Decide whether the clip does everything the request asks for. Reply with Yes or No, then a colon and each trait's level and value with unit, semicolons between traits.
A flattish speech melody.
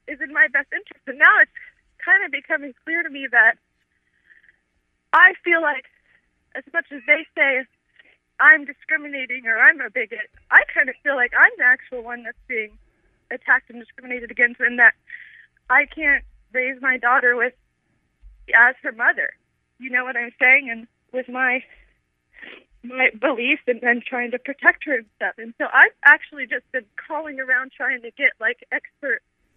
No: average, 3.4 semitones